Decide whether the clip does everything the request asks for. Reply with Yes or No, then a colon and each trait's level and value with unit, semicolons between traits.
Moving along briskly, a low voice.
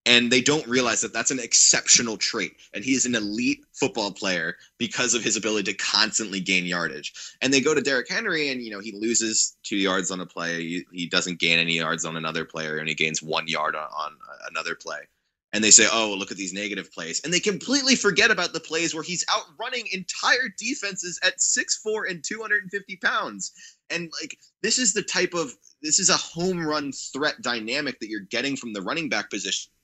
Yes: fast, 215 wpm; low, 130 Hz